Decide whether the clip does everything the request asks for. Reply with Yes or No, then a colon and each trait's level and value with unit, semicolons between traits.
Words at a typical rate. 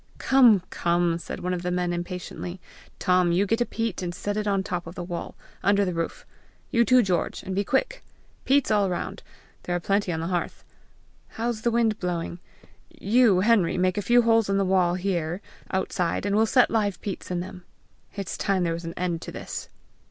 No: fast, 210 wpm